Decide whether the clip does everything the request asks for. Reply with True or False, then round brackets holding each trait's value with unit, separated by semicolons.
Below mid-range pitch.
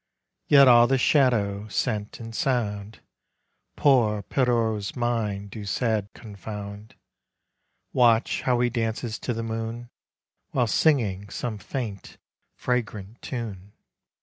True (115 Hz)